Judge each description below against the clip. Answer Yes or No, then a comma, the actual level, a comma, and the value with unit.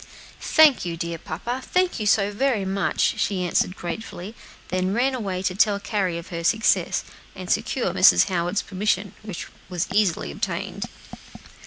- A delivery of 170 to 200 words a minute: No, average, 160 wpm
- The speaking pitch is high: Yes, high, 195 Hz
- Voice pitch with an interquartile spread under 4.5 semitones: Yes, average, 3.4 semitones